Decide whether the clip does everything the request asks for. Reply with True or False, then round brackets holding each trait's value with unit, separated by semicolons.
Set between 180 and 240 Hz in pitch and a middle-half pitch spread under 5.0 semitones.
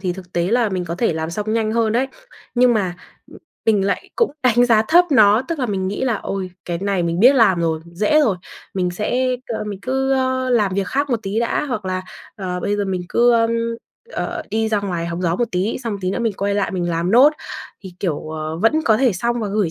True (210 Hz; 4.6 semitones)